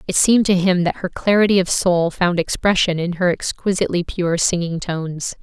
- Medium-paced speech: Yes, average, 190 wpm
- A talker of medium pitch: Yes, medium, 180 Hz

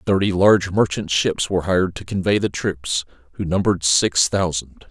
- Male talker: Yes, male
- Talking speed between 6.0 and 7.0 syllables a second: No, 5.2 syllables/s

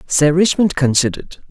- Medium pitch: Yes, medium, 160 Hz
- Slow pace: Yes, slow, 120 wpm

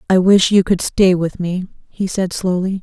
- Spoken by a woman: Yes, female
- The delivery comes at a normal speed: No, fast, 215 wpm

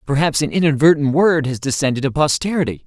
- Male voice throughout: Yes, male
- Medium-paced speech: Yes, average, 170 wpm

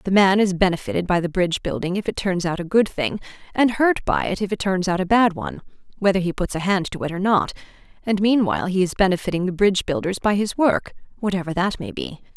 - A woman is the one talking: Yes, female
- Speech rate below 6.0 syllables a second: No, 6.2 syllables/s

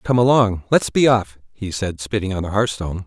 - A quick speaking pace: Yes, fast, 215 wpm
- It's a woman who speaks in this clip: No, male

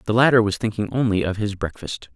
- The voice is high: No, low, 105 Hz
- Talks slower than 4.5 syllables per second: No, 6.0 syllables/s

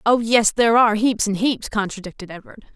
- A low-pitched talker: No, high, 220 Hz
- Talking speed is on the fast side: No, average, 195 wpm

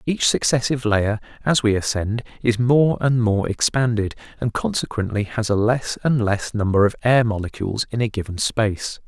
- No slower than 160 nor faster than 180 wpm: Yes, average, 170 wpm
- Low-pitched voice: Yes, low, 115 Hz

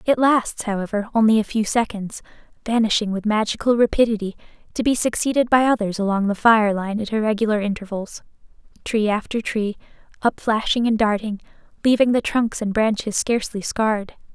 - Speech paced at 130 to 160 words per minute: Yes, average, 150 wpm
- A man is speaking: No, female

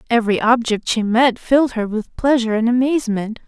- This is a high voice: Yes, high, 235 Hz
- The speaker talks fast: No, average, 175 wpm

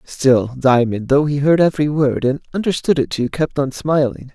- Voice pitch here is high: No, medium, 140 Hz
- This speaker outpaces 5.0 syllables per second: No, 4.9 syllables/s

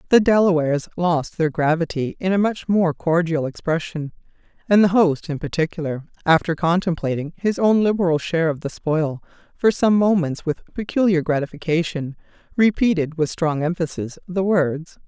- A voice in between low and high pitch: Yes, medium, 170 Hz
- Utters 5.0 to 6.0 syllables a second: Yes, 5.1 syllables/s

